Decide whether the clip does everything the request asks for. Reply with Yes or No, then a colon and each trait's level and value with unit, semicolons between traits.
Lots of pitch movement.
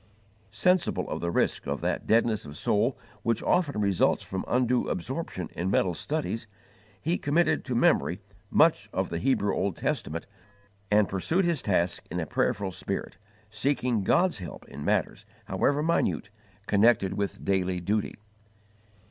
Yes: wide, 6.0 semitones